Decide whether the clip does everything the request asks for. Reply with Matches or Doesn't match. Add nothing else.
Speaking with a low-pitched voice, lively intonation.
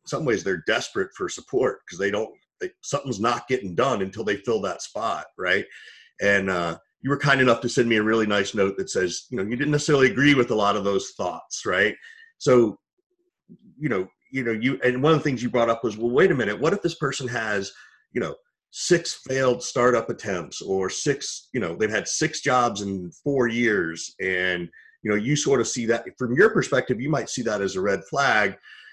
Matches